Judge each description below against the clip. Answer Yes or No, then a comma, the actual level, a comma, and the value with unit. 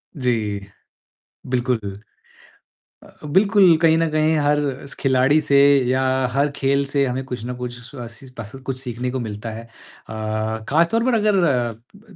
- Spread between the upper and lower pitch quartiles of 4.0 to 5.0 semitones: Yes, average, 4.3 semitones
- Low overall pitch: Yes, low, 130 Hz